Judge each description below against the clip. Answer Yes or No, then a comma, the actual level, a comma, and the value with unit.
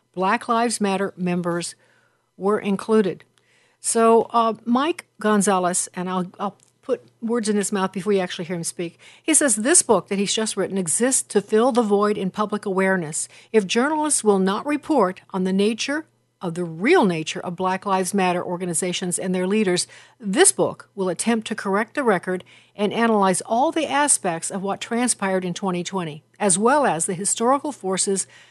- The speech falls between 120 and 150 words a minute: No, average, 175 wpm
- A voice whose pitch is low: No, high, 200 Hz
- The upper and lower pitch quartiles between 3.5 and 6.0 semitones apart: Yes, average, 3.8 semitones